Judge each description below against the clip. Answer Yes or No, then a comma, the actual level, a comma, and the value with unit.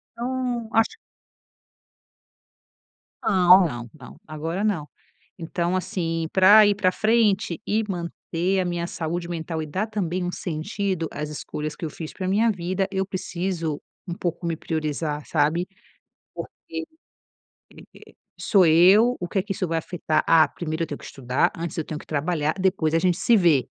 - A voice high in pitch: No, medium, 175 Hz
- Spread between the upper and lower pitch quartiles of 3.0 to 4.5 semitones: Yes, average, 3.3 semitones